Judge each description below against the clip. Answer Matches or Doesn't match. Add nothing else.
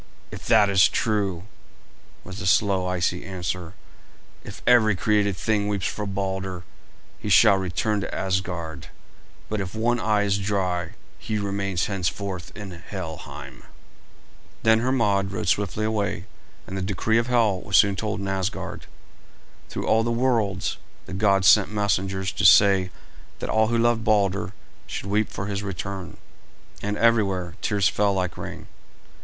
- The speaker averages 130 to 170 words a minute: Matches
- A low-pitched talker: Matches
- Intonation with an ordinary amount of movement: Doesn't match